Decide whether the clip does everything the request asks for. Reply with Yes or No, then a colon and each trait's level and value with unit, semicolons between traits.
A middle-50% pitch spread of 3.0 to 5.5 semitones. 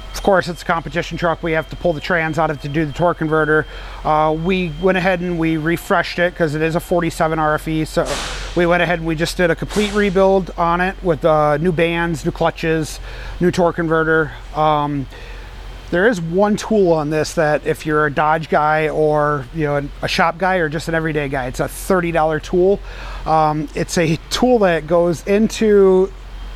No: narrow, 2.4 semitones